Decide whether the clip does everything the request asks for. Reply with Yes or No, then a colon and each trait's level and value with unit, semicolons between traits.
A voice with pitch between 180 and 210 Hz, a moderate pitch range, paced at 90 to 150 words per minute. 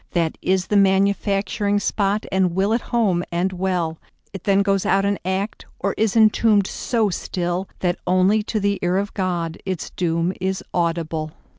No: high, 190 Hz; narrow, 2.3 semitones; average, 145 wpm